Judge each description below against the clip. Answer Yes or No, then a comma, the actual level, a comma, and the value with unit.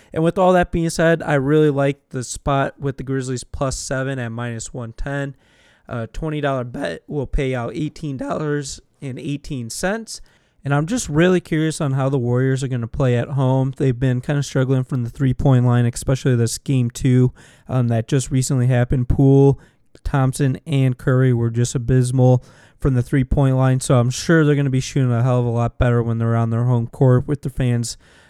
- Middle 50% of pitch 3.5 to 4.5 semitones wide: No, narrow, 2.4 semitones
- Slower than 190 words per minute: No, average, 200 wpm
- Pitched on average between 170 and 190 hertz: No, low, 135 Hz